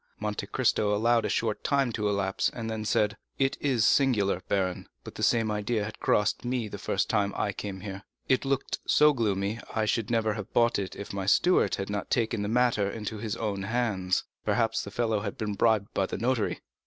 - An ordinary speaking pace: No, fast, 210 wpm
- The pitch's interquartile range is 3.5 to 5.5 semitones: No, narrow, 2.6 semitones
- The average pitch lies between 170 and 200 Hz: No, low, 110 Hz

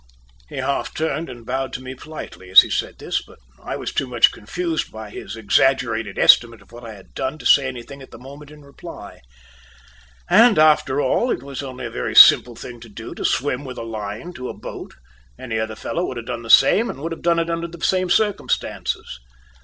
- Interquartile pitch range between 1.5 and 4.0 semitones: No, average, 5.1 semitones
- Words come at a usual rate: No, fast, 220 wpm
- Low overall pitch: Yes, low, 130 Hz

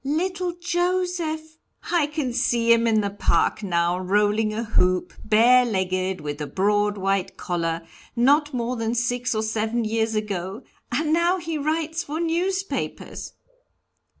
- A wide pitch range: Yes, wide, 7.6 semitones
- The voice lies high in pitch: Yes, high, 235 Hz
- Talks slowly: No, average, 145 wpm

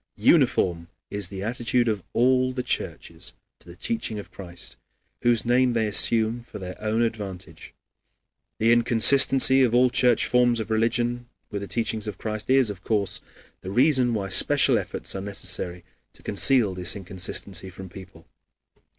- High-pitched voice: No, low, 110 Hz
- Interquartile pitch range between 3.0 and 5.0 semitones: Yes, average, 3.9 semitones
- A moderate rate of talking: Yes, average, 160 wpm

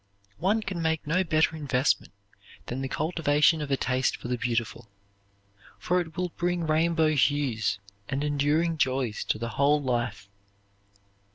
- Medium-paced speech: Yes, average, 150 wpm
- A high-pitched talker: No, medium, 145 Hz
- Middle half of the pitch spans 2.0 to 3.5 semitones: No, average, 4.2 semitones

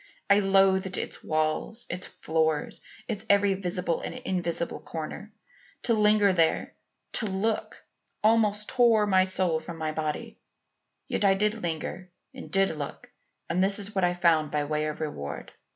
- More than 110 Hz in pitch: Yes, high, 190 Hz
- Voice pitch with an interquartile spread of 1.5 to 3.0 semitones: No, average, 4.4 semitones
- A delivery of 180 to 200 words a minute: No, average, 155 wpm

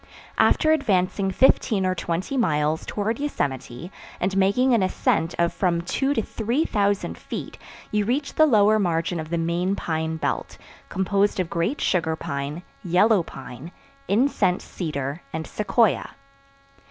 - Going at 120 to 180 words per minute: Yes, average, 140 wpm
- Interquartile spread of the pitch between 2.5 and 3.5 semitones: No, average, 4.6 semitones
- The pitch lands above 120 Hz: Yes, medium, 185 Hz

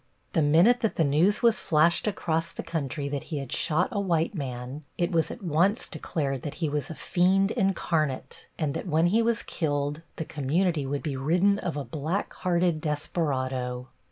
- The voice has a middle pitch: Yes, medium, 160 Hz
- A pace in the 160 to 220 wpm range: Yes, average, 185 wpm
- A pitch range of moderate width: Yes, average, 3.9 semitones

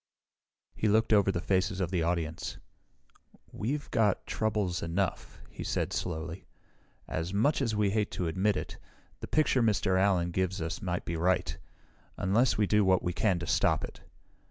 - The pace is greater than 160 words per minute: Yes, average, 170 wpm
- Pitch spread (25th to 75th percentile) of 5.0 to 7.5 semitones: No, average, 3.3 semitones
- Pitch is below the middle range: Yes, very low, 95 Hz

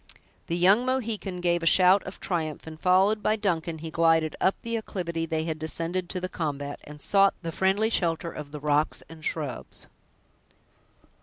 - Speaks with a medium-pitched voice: Yes, medium, 170 Hz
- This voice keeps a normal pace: Yes, average, 175 wpm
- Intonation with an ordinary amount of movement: Yes, average, 3.3 semitones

